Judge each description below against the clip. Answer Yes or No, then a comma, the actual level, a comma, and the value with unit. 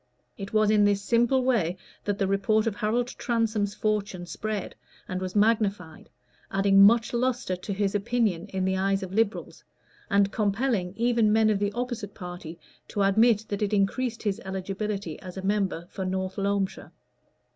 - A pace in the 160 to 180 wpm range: Yes, average, 165 wpm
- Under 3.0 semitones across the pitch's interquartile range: Yes, narrow, 2.4 semitones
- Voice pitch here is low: No, high, 205 Hz